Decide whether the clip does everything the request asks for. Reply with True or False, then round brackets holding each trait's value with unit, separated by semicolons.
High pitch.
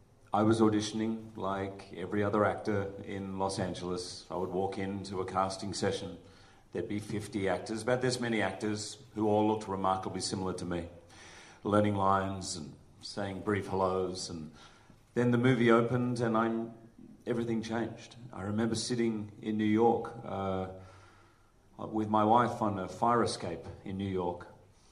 False (105 Hz)